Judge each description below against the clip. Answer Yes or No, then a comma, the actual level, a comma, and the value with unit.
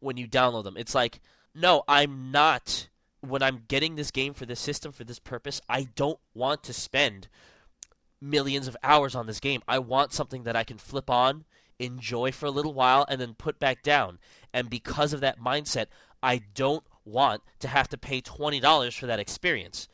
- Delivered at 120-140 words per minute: No, average, 195 wpm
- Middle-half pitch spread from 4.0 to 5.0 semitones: No, average, 2.7 semitones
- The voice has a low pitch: Yes, low, 130 Hz